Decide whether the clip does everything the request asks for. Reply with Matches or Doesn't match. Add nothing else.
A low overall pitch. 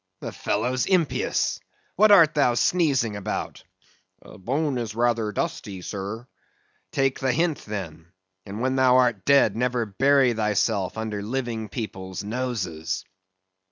Matches